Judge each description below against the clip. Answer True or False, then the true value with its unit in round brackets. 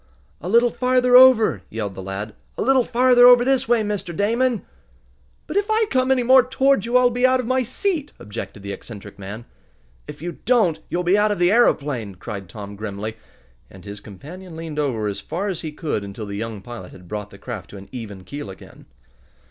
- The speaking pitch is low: False (165 Hz)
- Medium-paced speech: False (210 wpm)